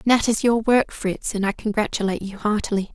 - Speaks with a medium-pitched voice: No, high, 210 Hz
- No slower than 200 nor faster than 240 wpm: Yes, fast, 205 wpm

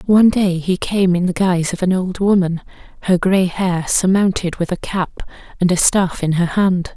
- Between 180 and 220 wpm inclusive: Yes, fast, 205 wpm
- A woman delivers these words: Yes, female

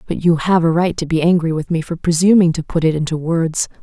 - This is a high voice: No, medium, 165 Hz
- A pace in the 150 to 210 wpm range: No, fast, 265 wpm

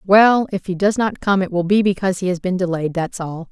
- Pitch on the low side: No, high, 190 Hz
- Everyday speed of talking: No, fast, 275 wpm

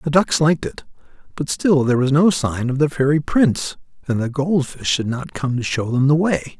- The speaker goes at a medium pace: No, fast, 235 wpm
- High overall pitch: No, medium, 140 Hz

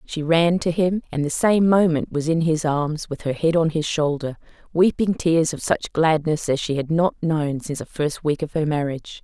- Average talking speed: No, fast, 225 wpm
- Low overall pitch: No, medium, 160 Hz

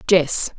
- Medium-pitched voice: Yes, medium, 170 Hz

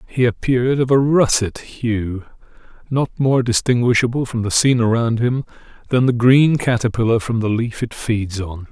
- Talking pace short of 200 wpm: Yes, average, 165 wpm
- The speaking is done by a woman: No, male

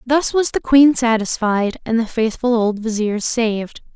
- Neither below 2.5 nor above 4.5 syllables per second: Yes, 4.3 syllables/s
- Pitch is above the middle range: Yes, high, 235 Hz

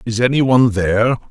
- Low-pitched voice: Yes, low, 115 Hz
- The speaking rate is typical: Yes, average, 185 wpm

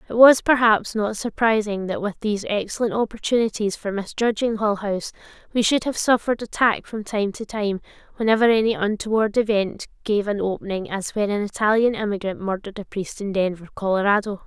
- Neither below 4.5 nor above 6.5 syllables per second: Yes, 5.7 syllables/s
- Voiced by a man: No, female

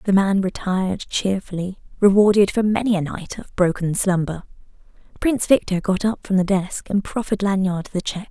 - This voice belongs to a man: No, female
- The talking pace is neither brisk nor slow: Yes, average, 175 wpm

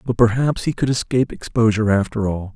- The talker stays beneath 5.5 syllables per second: No, 6.2 syllables/s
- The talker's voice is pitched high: No, low, 115 Hz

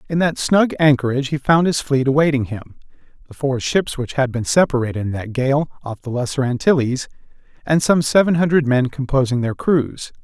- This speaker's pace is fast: No, average, 180 wpm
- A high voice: No, low, 135 Hz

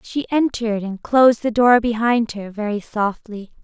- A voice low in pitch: No, high, 225 Hz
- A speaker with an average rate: Yes, average, 165 wpm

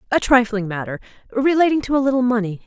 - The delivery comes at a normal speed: Yes, average, 180 wpm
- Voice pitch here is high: Yes, high, 240 Hz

